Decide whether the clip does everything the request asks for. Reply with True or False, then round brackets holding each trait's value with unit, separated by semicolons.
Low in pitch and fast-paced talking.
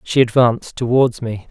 False (120 Hz; 160 wpm)